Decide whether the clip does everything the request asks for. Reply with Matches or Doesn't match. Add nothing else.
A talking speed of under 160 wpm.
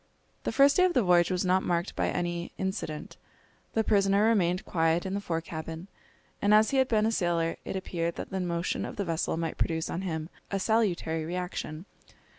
Doesn't match